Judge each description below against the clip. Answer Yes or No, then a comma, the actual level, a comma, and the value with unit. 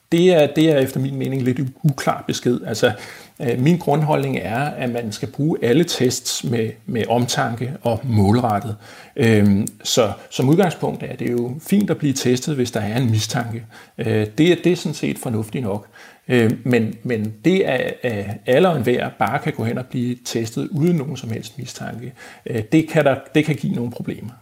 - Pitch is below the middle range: Yes, low, 125 Hz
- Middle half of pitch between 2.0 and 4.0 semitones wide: No, average, 4.4 semitones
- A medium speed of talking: Yes, average, 205 wpm